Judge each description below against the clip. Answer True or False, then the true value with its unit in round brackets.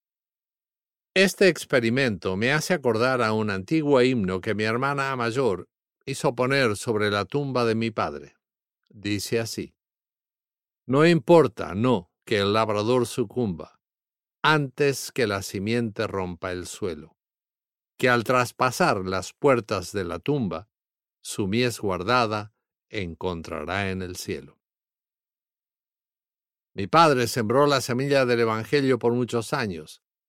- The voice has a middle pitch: False (120 Hz)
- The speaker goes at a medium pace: False (125 wpm)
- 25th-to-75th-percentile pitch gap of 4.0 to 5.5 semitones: True (4.4 semitones)